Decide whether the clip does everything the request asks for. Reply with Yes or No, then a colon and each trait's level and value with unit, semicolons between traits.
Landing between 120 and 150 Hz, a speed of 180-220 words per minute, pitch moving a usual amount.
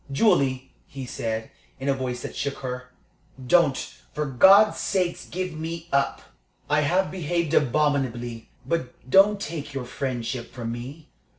No: medium, 140 Hz; average, 140 wpm; average, 4.9 semitones